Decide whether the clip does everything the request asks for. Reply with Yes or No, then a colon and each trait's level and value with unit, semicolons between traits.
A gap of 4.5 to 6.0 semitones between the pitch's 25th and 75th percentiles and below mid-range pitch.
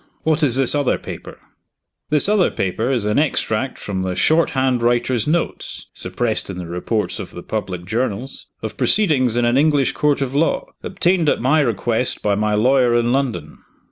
Yes: average, 5.1 semitones; low, 125 Hz